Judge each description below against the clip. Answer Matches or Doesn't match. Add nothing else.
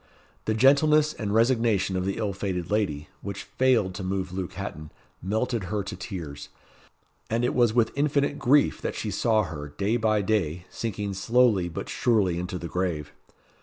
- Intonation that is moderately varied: Matches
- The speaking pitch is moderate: Doesn't match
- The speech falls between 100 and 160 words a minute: Doesn't match